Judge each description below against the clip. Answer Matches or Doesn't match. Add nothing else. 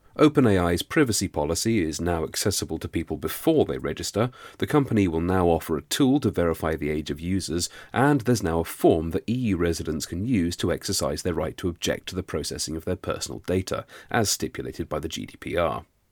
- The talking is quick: Doesn't match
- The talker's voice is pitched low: Matches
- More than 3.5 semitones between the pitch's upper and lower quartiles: Matches